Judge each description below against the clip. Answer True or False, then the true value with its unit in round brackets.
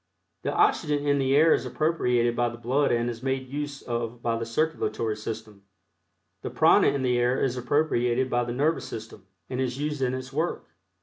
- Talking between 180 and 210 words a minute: True (195 wpm)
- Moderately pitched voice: False (125 Hz)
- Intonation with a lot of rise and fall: False (3.4 semitones)